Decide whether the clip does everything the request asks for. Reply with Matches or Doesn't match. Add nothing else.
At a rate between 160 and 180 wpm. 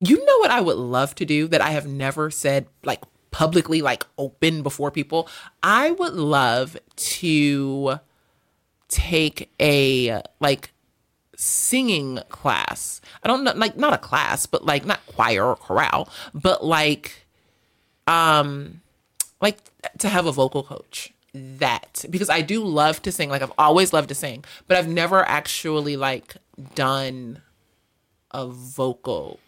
Doesn't match